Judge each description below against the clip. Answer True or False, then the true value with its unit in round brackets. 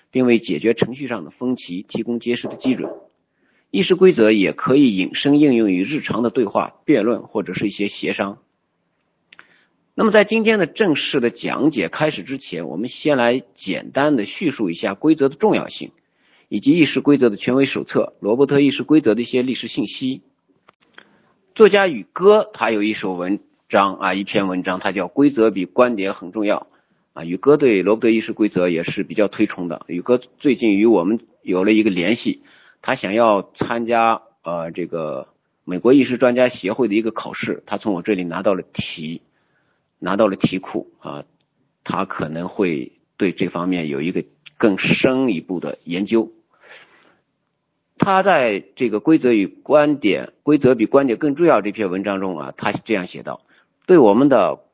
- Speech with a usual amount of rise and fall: False (6.7 semitones)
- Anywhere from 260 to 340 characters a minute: True (265 characters per minute)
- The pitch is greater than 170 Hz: False (120 Hz)